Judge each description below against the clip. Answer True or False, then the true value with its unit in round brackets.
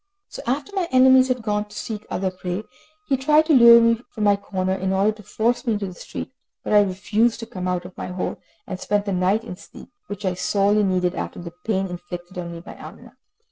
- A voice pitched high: True (205 Hz)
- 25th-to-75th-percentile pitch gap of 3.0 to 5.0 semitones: True (3.9 semitones)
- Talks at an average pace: False (235 wpm)